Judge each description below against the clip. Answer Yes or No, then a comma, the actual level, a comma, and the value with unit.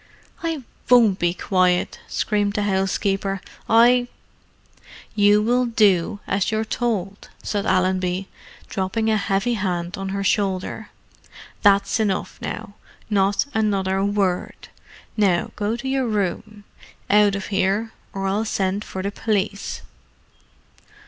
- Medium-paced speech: No, slow, 120 wpm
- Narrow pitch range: Yes, narrow, 2.1 semitones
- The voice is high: Yes, high, 200 Hz